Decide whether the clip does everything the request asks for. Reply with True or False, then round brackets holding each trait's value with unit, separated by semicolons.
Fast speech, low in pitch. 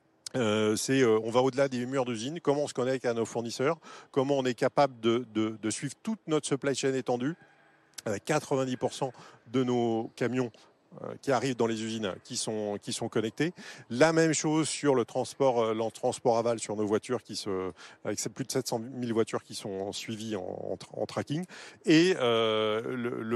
False (200 wpm; 125 Hz)